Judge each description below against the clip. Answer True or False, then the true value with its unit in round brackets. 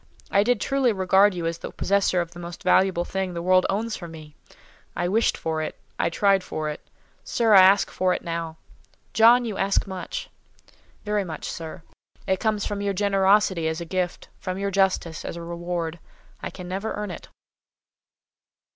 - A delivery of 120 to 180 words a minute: False (190 wpm)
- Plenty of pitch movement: False (2.9 semitones)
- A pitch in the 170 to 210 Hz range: True (185 Hz)